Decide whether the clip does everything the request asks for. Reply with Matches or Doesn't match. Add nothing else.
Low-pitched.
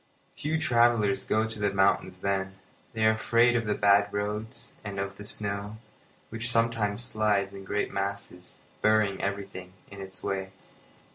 Matches